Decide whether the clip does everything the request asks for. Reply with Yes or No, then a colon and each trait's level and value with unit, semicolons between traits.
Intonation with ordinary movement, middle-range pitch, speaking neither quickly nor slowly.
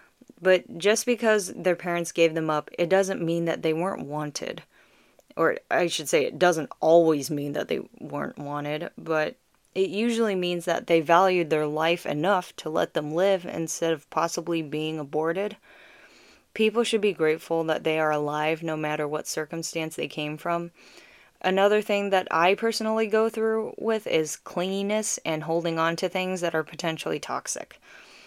Yes: average, 3.5 semitones; medium, 170 Hz; average, 170 wpm